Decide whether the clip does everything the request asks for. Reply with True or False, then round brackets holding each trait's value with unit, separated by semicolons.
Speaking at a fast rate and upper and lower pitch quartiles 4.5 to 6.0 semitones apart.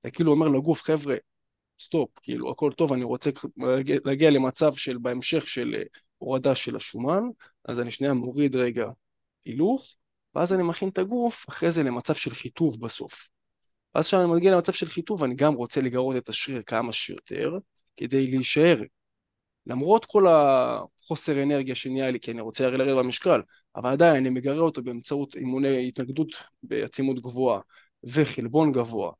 False (155 wpm; 3.9 semitones)